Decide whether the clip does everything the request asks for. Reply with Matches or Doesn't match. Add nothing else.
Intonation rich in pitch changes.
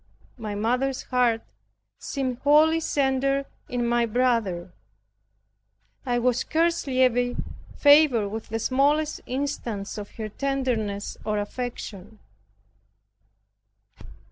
Doesn't match